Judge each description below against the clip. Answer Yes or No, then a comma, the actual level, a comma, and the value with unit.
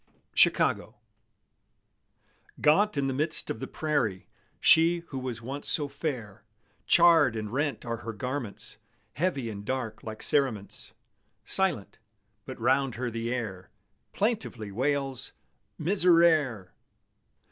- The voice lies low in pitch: Yes, low, 130 Hz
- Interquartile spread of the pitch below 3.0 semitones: No, average, 5.3 semitones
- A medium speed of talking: No, slow, 115 wpm